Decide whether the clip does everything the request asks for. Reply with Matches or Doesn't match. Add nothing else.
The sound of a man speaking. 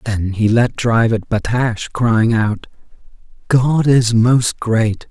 Matches